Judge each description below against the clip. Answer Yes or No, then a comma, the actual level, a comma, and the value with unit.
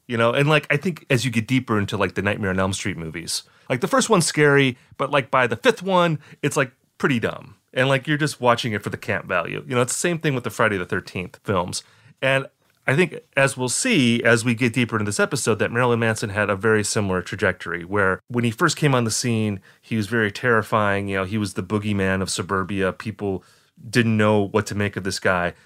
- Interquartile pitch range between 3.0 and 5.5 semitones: Yes, average, 4.5 semitones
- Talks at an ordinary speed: No, fast, 245 wpm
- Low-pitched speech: Yes, low, 120 Hz